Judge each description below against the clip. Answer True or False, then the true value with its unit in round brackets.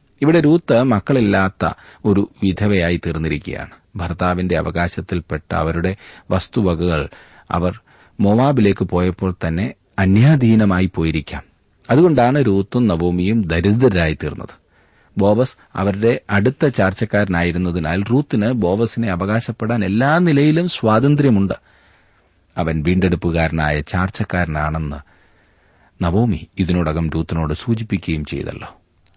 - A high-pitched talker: False (95 Hz)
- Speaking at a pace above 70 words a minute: True (80 wpm)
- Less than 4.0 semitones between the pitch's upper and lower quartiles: False (4.9 semitones)